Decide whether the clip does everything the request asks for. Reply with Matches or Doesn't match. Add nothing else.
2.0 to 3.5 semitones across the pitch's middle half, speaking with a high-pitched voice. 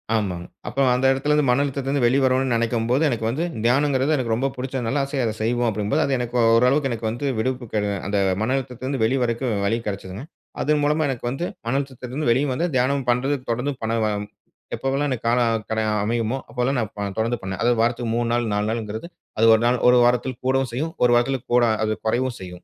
Doesn't match